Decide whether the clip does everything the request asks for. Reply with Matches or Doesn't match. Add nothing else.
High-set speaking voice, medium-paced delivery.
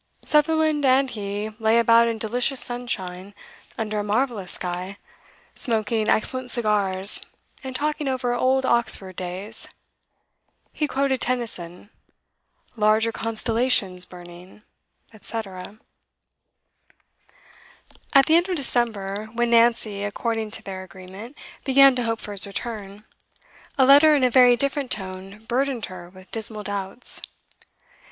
Doesn't match